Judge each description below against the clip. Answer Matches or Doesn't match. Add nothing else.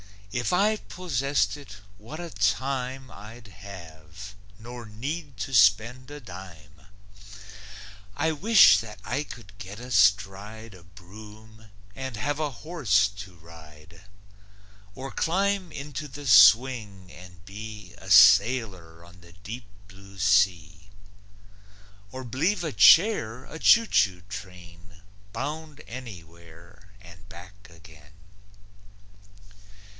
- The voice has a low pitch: Matches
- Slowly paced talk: Matches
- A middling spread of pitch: Doesn't match